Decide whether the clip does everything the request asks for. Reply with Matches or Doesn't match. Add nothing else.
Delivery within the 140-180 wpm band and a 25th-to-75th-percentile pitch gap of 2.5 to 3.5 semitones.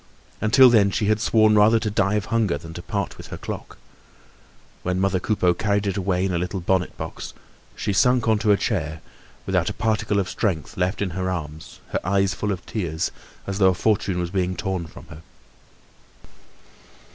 Doesn't match